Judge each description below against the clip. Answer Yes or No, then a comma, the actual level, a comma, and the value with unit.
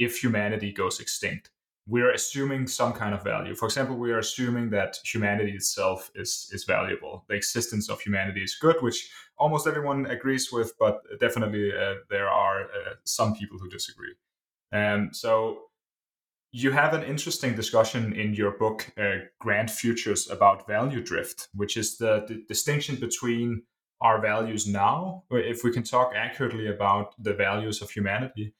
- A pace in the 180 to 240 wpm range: No, average, 165 wpm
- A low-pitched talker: Yes, low, 115 Hz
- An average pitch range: Yes, average, 3.7 semitones